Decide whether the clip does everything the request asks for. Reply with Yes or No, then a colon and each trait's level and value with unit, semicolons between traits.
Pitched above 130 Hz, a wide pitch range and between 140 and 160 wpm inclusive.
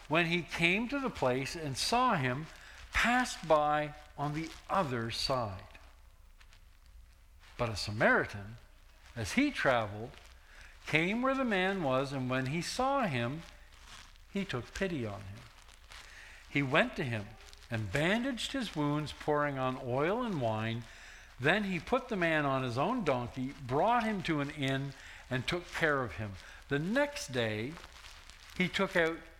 Yes: medium, 140 Hz; wide, 7.9 semitones; average, 150 wpm